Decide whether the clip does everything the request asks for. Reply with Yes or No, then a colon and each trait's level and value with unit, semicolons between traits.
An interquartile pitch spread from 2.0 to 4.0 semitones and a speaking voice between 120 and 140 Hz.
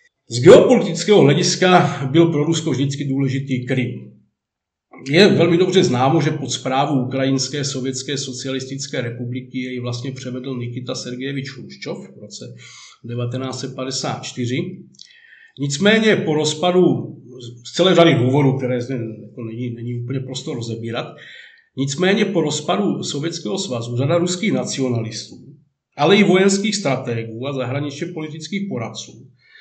No: average, 4.7 semitones; low, 135 Hz